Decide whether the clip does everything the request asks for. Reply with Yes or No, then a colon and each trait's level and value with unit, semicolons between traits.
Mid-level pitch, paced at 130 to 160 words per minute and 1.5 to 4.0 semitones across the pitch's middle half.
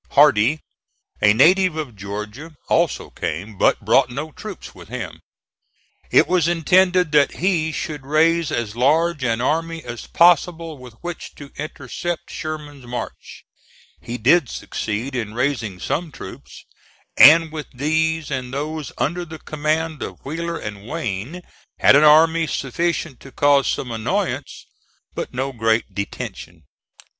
No: medium, 150 Hz; average, 140 wpm; average, 4.8 semitones